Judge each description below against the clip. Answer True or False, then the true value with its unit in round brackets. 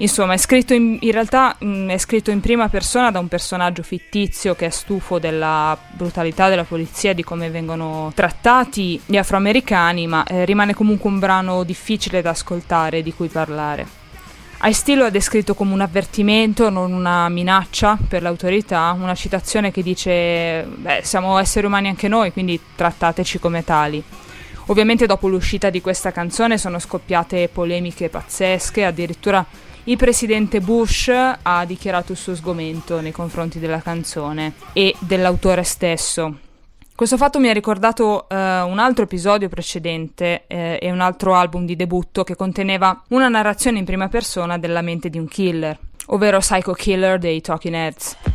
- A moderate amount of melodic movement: True (3.2 semitones)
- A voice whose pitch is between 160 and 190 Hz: True (185 Hz)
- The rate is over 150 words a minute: True (160 wpm)